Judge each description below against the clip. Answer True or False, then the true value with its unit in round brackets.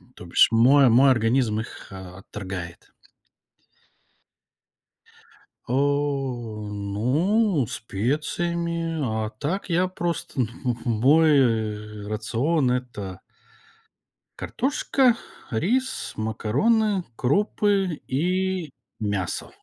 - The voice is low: True (130 Hz)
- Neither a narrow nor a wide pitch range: False (7.7 semitones)